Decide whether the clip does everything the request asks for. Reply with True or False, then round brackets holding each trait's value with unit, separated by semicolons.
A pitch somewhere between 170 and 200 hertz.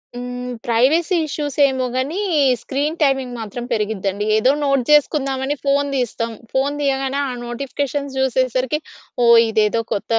False (265 Hz)